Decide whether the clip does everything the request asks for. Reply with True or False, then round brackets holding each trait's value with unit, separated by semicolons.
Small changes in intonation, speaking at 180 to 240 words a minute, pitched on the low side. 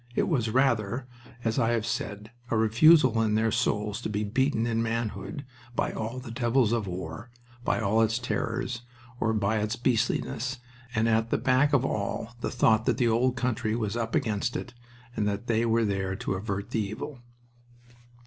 True (2.2 semitones; 185 wpm; 115 Hz)